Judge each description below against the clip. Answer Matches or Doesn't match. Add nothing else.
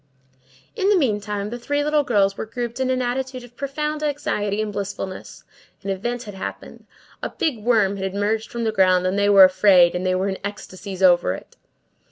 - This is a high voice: Matches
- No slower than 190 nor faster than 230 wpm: Matches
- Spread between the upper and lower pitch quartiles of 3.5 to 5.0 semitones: Matches